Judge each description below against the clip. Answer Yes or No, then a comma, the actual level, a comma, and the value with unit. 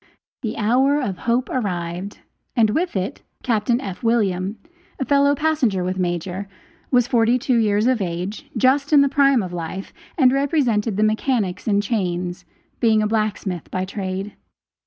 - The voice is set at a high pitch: Yes, high, 215 Hz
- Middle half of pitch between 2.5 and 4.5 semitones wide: No, average, 5.3 semitones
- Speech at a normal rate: Yes, average, 155 wpm